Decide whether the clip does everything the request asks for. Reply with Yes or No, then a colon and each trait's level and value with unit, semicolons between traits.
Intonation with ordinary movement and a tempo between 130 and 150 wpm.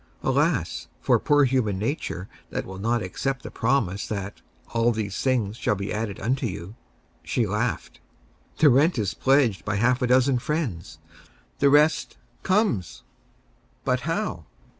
Yes: average, 5.0 semitones; average, 145 wpm